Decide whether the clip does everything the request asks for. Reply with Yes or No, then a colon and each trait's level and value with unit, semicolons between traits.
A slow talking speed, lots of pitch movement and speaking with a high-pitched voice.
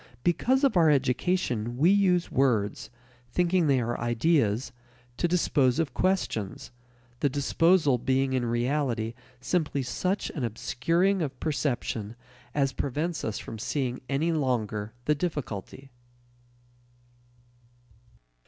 No: slow, 115 wpm; wide, 5.8 semitones; medium, 140 Hz